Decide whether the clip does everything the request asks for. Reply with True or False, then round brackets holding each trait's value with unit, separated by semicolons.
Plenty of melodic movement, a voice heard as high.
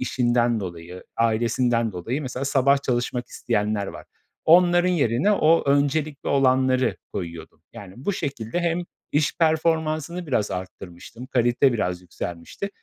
False (6.0 semitones; 125 Hz)